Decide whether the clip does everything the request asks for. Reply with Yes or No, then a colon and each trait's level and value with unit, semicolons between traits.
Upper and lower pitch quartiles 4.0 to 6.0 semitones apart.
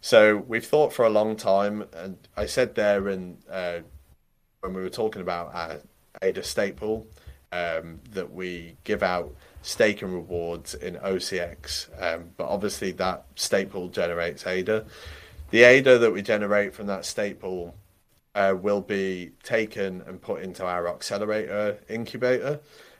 No: average, 3.5 semitones